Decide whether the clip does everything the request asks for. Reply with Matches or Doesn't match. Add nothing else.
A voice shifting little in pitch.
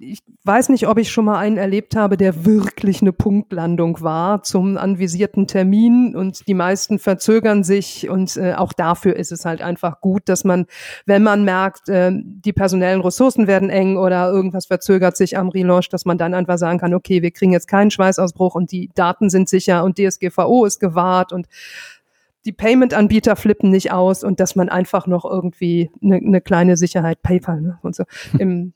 Matches